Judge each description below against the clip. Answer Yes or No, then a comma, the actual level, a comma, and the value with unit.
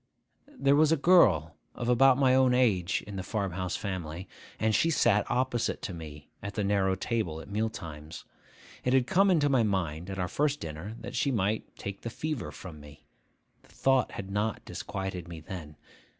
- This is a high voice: No, low, 100 Hz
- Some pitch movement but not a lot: No, wide, 6.2 semitones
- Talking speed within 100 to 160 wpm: No, average, 195 wpm